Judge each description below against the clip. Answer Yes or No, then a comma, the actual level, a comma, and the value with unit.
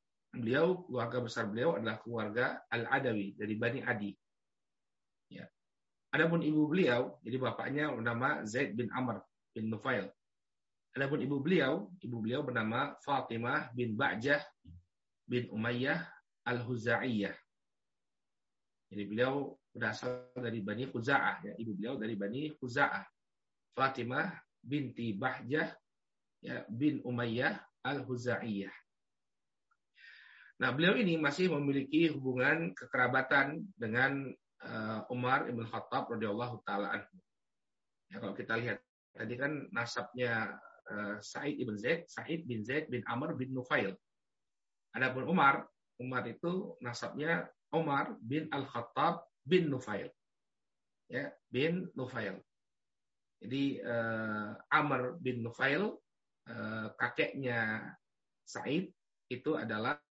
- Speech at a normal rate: Yes, average, 105 wpm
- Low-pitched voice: Yes, low, 125 Hz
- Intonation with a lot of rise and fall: No, average, 3.5 semitones